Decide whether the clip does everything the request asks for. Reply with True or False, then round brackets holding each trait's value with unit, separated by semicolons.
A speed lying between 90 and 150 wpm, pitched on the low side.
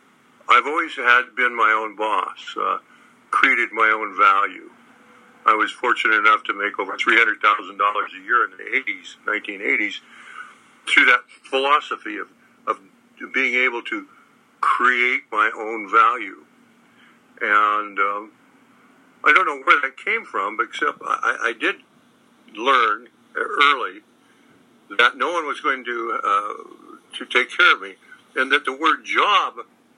False (140 wpm; 390 Hz)